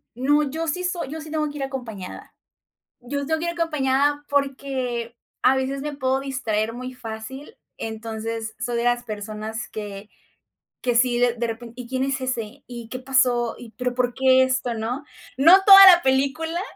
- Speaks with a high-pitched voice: Yes, very high, 255 Hz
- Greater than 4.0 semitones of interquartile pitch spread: No, average, 3.1 semitones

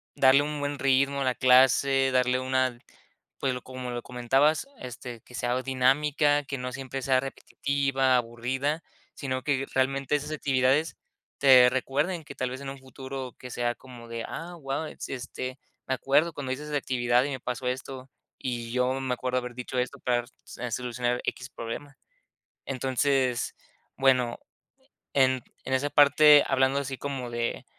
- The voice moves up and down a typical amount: No, narrow, 1.6 semitones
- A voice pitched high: No, low, 130 Hz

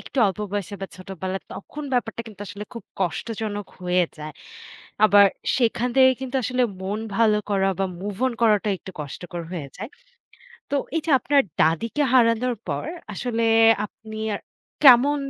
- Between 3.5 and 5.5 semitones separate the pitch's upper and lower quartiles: Yes, average, 4.1 semitones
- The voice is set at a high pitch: Yes, high, 210 Hz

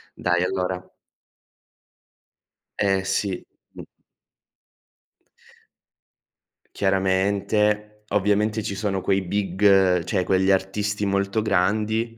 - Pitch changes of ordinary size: No, narrow, 1.8 semitones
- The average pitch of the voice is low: Yes, low, 100 Hz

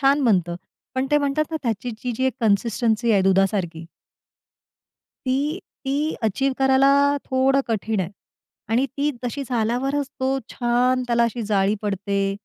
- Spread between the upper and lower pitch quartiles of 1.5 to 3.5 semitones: No, average, 4.5 semitones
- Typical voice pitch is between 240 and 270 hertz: Yes, high, 245 Hz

